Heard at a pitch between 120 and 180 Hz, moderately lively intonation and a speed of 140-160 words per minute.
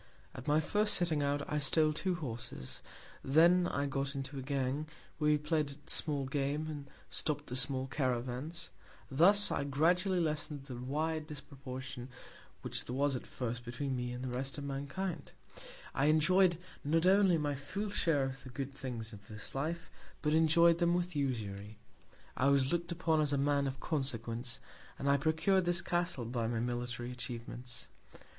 No: medium, 140 Hz; average, 3.8 semitones; average, 175 wpm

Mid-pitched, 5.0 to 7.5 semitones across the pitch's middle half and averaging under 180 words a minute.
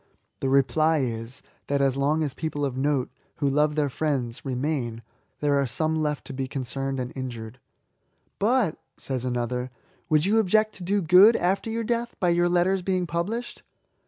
No: medium, 150 Hz; average, 5.3 semitones; average, 185 wpm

